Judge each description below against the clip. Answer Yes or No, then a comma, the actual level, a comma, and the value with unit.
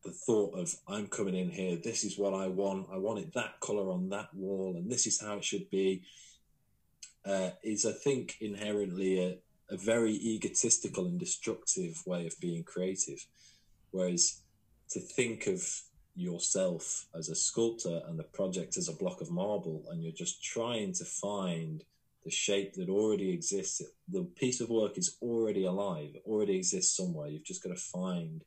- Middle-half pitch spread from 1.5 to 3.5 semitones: No, average, 4.1 semitones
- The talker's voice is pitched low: Yes, low, 100 Hz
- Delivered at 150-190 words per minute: Yes, average, 180 wpm